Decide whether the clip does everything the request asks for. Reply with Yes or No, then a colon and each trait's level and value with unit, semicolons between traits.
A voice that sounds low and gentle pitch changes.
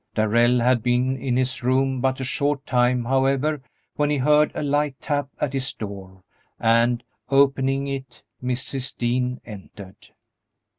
Yes: low, 130 Hz; narrow, 2.1 semitones